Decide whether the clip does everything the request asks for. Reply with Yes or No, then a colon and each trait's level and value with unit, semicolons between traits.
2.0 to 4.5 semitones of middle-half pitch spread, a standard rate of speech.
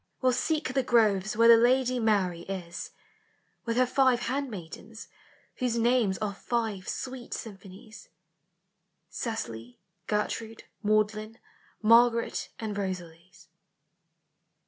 No: average, 3.7 semitones; slow, 110 wpm